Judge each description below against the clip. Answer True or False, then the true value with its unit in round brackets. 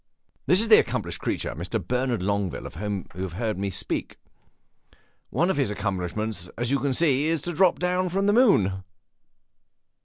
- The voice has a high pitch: False (115 Hz)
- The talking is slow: False (175 wpm)